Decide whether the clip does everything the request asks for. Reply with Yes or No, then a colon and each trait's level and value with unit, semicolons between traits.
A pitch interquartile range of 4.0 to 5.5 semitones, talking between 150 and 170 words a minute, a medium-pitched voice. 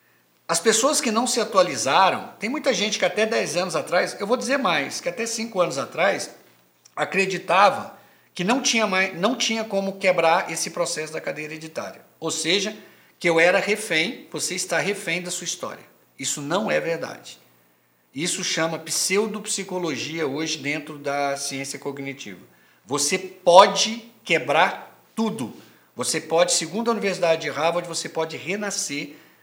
Yes: average, 5.0 semitones; average, 155 wpm; medium, 180 Hz